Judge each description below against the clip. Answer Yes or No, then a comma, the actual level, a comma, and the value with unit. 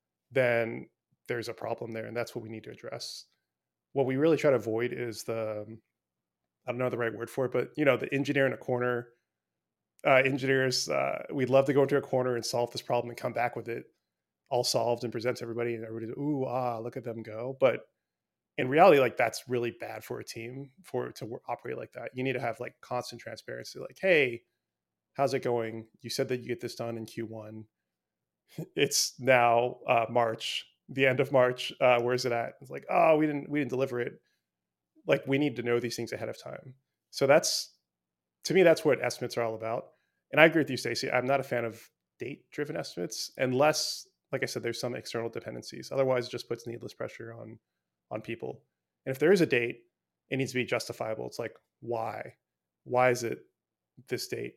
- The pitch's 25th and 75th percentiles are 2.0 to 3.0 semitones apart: Yes, narrow, 2.5 semitones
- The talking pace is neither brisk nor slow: No, fast, 220 wpm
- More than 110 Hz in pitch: Yes, low, 120 Hz